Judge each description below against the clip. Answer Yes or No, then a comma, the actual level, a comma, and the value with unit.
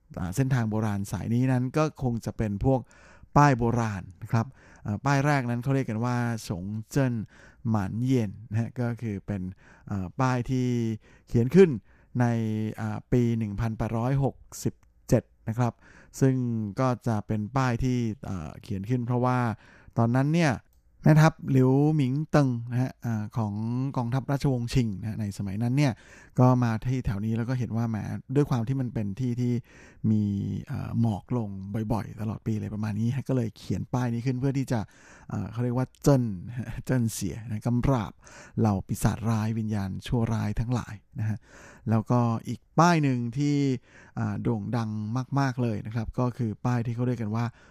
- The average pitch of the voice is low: Yes, low, 115 Hz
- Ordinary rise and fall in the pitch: Yes, average, 3.0 semitones